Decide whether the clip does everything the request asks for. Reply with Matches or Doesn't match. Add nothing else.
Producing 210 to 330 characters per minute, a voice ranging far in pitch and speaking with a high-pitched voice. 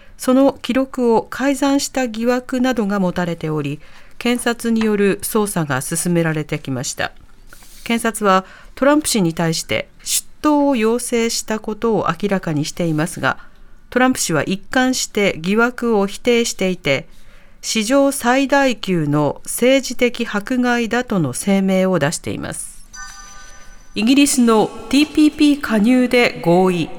Matches